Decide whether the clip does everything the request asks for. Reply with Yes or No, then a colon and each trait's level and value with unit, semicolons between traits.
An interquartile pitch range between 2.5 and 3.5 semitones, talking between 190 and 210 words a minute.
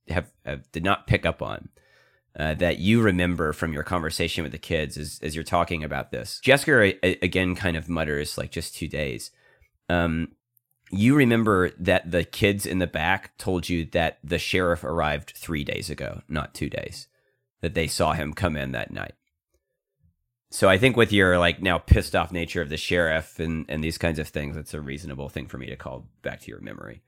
Yes: average, 2.9 semitones; fast, 205 wpm